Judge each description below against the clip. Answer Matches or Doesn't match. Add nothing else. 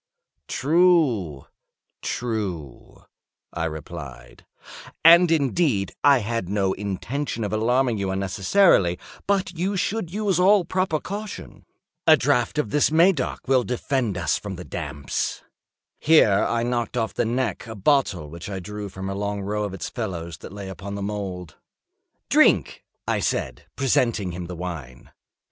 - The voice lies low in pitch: Matches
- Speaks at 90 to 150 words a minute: Matches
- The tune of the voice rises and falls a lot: Matches